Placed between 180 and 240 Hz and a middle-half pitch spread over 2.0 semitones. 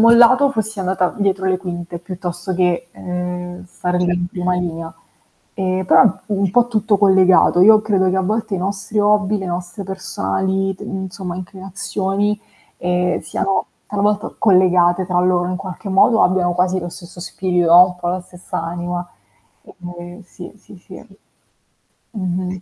No: medium, 185 Hz; narrow, 1.7 semitones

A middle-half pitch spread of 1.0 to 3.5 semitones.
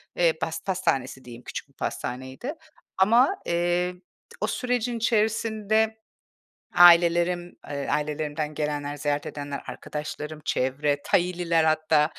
No: average, 4.3 semitones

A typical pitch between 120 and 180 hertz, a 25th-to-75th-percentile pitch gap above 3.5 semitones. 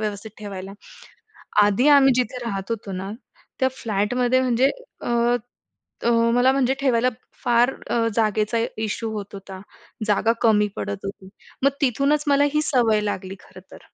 No: high, 230 Hz; average, 4.0 semitones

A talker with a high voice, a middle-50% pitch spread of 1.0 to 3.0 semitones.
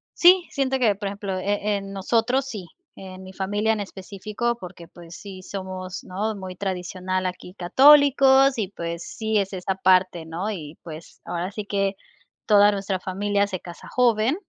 Yes: high, 195 Hz; average, 2.7 semitones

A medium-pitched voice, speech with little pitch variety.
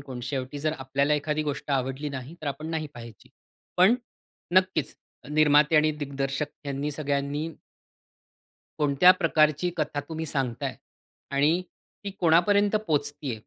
Yes: medium, 150 Hz; narrow, 2.1 semitones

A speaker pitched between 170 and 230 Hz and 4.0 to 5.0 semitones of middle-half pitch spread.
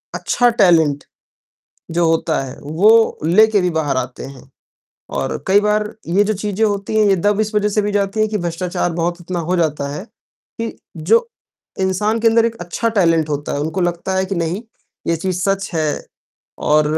Yes: medium, 185 Hz; average, 4.3 semitones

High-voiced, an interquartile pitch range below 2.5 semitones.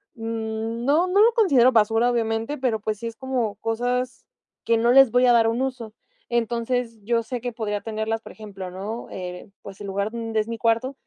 Yes: high, 230 Hz; narrow, 2.1 semitones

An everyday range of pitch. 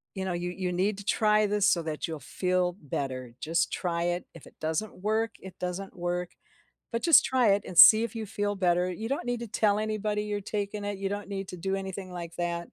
Yes: average, 3.1 semitones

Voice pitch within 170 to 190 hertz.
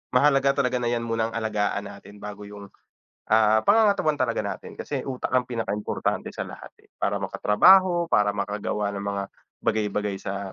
No: low, 110 Hz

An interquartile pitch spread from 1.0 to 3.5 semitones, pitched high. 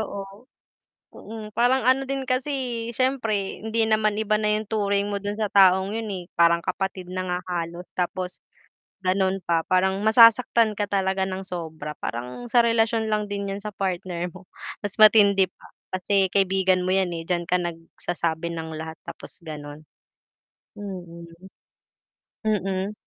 Yes: average, 3.2 semitones; high, 195 Hz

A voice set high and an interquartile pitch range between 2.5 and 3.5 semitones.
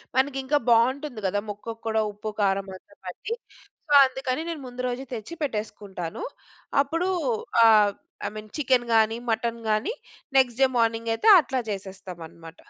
No: high, 230 Hz; average, 4.1 semitones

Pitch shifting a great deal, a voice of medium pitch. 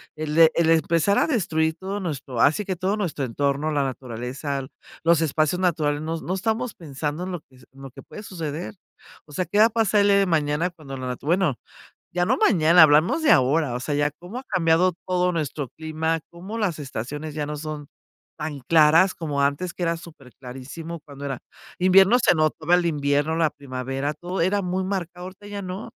No: average, 3.9 semitones; medium, 160 Hz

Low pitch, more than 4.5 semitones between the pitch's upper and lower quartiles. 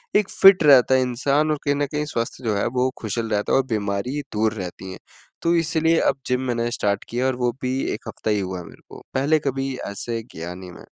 Yes: low, 125 Hz; average, 5.2 semitones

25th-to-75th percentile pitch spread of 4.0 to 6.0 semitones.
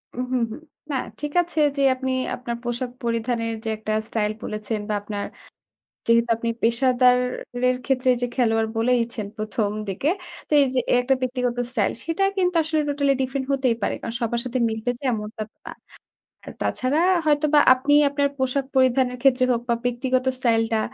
No: narrow, 2.6 semitones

